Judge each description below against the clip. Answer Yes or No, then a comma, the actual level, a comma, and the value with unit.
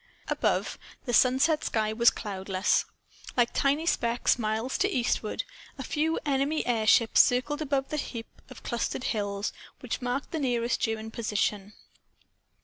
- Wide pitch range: No, average, 4.0 semitones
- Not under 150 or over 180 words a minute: No, average, 140 wpm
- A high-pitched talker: Yes, high, 240 Hz